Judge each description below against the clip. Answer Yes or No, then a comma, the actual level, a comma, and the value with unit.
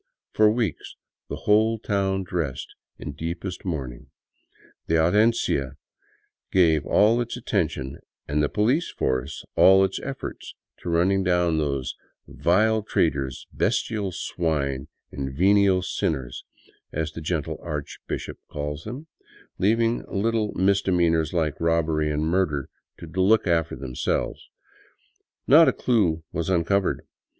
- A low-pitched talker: Yes, very low, 85 Hz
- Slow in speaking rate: Yes, slow, 125 wpm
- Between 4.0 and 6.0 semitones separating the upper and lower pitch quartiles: Yes, average, 4.8 semitones